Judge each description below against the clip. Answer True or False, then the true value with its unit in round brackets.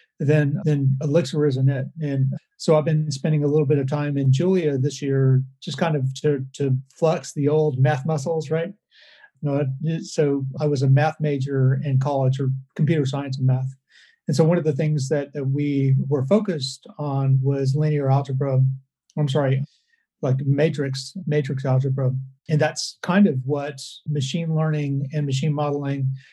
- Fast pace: False (175 wpm)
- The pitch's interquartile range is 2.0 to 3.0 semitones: True (2.4 semitones)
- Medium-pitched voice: True (145 Hz)